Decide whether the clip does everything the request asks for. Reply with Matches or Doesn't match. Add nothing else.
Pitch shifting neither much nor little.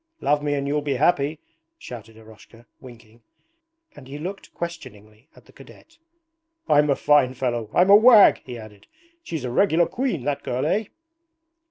Doesn't match